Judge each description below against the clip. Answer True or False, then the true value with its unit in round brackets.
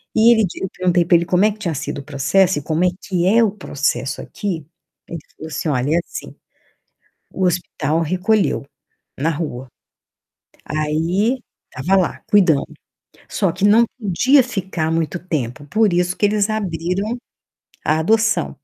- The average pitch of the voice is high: False (180 Hz)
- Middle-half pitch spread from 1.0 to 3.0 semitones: False (4.7 semitones)